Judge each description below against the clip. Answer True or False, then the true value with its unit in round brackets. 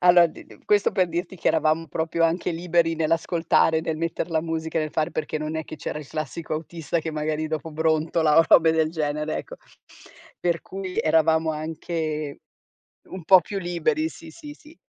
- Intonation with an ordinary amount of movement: False (1.7 semitones)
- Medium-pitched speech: True (160 Hz)